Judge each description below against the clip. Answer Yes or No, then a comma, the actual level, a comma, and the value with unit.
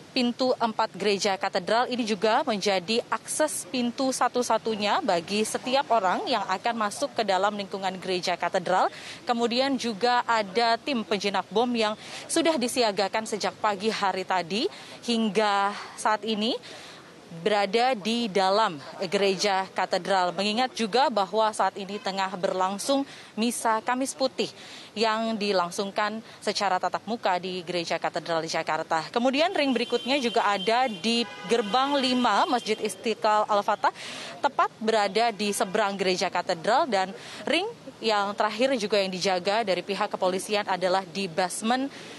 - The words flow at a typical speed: Yes, average, 130 wpm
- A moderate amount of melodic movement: Yes, average, 3.6 semitones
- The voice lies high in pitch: Yes, high, 215 Hz